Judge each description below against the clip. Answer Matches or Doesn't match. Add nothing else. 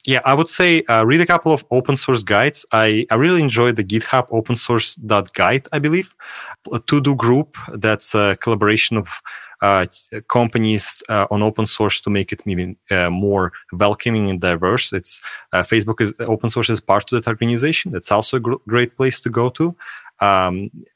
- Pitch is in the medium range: Doesn't match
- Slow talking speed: Doesn't match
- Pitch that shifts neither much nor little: Matches